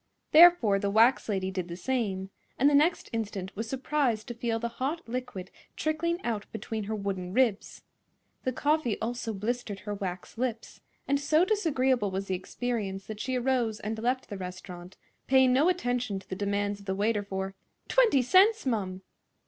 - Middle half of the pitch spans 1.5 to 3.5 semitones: No, average, 4.8 semitones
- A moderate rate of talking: Yes, average, 175 wpm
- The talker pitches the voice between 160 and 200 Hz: No, high, 225 Hz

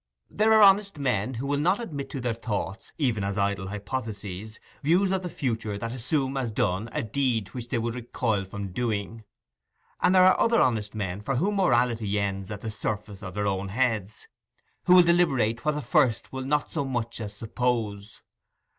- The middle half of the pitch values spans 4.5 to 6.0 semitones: Yes, average, 5.2 semitones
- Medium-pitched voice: No, low, 115 Hz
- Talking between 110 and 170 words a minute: No, average, 190 wpm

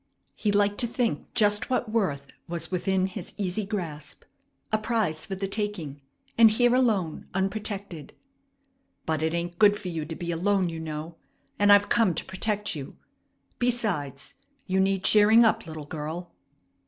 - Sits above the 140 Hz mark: Yes, high, 190 Hz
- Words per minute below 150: No, average, 160 wpm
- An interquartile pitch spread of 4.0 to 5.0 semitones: Yes, average, 4.5 semitones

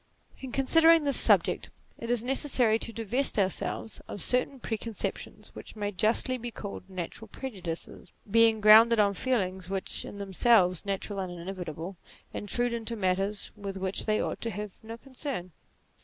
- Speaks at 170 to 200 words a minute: No, average, 155 wpm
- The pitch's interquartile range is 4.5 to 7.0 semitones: No, average, 3.8 semitones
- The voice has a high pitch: Yes, high, 215 Hz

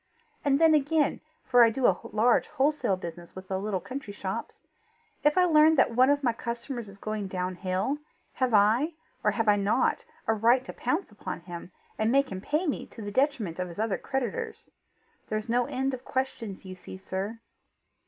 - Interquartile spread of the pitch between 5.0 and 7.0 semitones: Yes, wide, 5.6 semitones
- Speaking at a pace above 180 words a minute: Yes, average, 195 wpm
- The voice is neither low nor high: No, high, 230 Hz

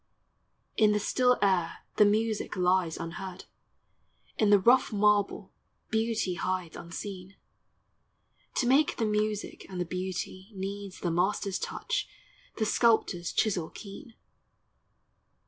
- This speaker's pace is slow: Yes, slow, 115 wpm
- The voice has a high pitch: Yes, high, 200 Hz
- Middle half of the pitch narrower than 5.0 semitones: Yes, average, 3.0 semitones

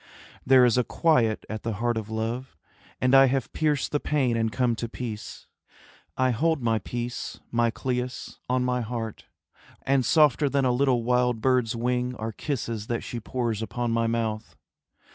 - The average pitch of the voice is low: Yes, low, 120 Hz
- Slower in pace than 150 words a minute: No, average, 175 wpm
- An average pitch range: No, narrow, 2.1 semitones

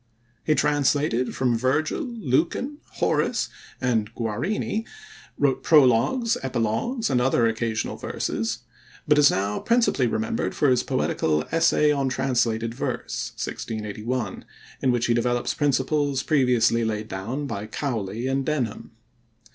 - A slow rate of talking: Yes, slow, 125 wpm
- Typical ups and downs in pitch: Yes, average, 4.4 semitones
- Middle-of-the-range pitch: No, low, 125 Hz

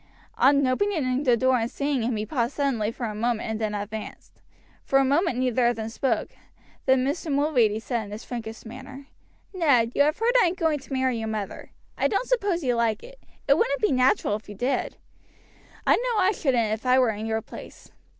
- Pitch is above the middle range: Yes, very high, 255 Hz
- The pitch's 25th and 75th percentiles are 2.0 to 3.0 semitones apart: No, average, 4.6 semitones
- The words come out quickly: Yes, fast, 220 wpm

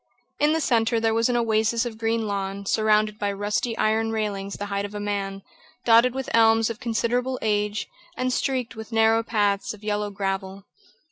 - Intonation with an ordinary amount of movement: No, narrow, 2.0 semitones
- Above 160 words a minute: Yes, average, 185 wpm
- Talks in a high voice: Yes, high, 220 Hz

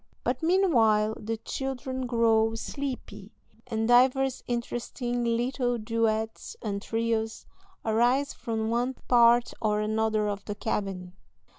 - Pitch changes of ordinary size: No, narrow, 2.1 semitones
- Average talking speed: No, slow, 115 wpm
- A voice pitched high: Yes, high, 230 Hz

